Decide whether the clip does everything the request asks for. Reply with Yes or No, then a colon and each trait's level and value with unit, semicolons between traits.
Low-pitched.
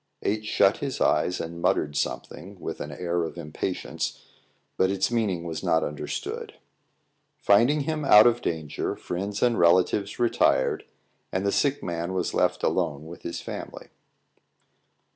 Yes: very low, 95 Hz